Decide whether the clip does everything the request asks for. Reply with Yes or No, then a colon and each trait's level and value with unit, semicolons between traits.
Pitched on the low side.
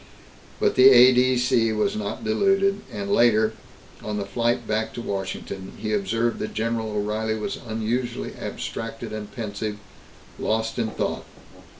Yes: low, 110 Hz